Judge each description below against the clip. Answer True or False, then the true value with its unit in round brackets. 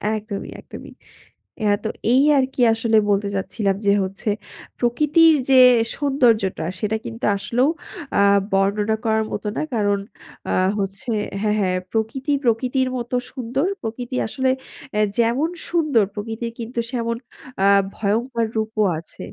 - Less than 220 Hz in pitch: False (230 Hz)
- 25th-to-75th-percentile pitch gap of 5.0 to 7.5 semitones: False (3.5 semitones)